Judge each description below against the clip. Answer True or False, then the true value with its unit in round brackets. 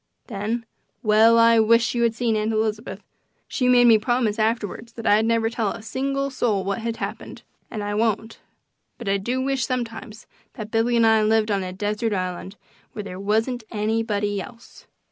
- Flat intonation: True (1.9 semitones)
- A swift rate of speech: False (180 wpm)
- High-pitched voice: True (225 Hz)